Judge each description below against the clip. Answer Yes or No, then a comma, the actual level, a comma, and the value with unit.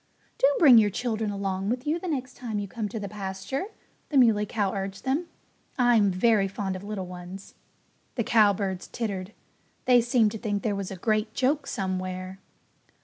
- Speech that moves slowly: No, average, 180 wpm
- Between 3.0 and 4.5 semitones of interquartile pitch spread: Yes, average, 3.9 semitones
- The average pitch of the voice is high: Yes, high, 210 Hz